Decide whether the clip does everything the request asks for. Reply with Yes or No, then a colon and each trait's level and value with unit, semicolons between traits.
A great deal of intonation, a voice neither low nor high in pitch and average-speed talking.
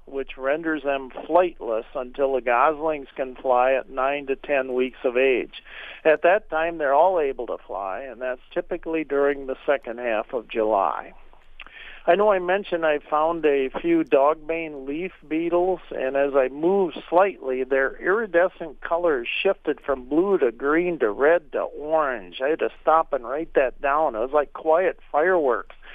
No: average, 4.5 semitones; medium, 155 Hz; average, 170 wpm